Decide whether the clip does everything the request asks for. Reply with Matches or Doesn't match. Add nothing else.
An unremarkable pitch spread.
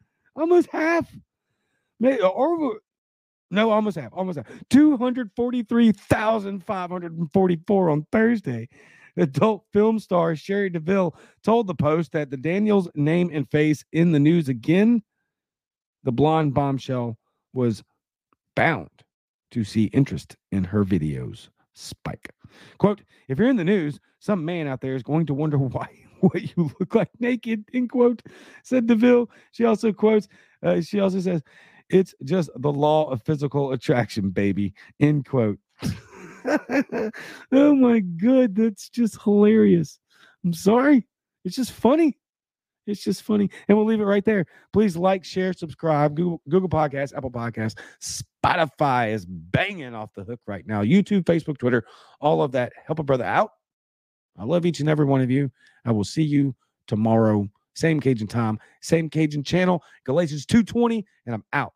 Doesn't match